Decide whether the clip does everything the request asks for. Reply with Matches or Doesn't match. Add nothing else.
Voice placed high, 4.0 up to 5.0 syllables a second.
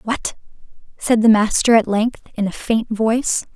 Matches